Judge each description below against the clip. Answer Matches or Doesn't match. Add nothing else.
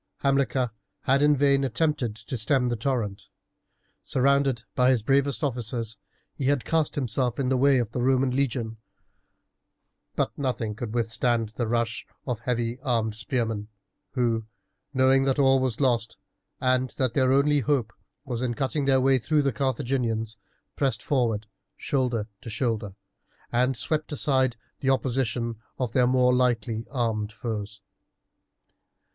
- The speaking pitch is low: Matches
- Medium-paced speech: Matches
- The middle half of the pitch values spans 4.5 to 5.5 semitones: Doesn't match